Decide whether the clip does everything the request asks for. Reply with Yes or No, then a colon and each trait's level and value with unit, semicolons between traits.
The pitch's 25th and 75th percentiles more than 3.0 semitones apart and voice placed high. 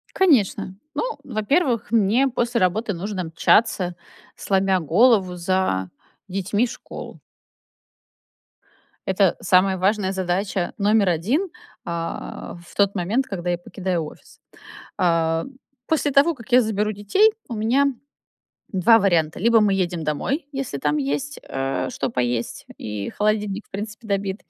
Yes: average, 4.3 semitones; high, 195 Hz